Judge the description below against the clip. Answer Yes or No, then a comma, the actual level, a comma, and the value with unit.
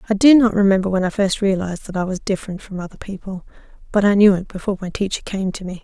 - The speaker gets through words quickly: Yes, fast, 255 wpm